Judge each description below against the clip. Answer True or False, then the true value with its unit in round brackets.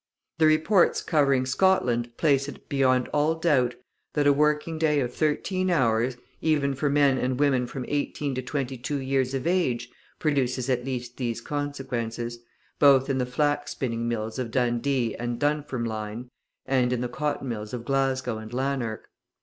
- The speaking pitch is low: True (130 Hz)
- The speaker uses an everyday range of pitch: True (3.1 semitones)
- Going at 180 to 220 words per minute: False (165 wpm)